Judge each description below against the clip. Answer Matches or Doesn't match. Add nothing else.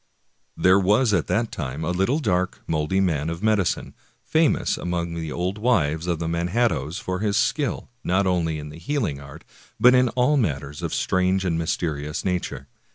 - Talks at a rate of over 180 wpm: Doesn't match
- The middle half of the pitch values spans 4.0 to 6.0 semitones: Matches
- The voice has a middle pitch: Doesn't match